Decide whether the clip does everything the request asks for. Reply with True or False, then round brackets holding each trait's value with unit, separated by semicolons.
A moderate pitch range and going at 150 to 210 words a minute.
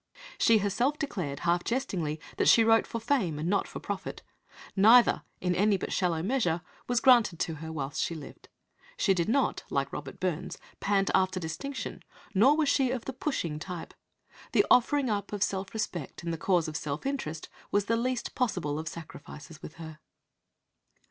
False (6.4 semitones; 180 wpm)